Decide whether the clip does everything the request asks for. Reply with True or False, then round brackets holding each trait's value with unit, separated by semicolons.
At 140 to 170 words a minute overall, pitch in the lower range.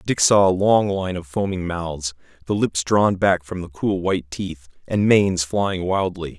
False (195 wpm; 90 Hz)